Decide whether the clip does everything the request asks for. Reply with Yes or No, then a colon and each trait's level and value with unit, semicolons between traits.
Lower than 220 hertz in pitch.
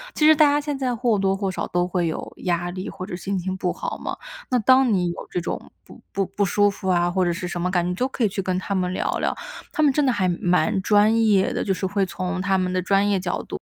Yes: high, 190 Hz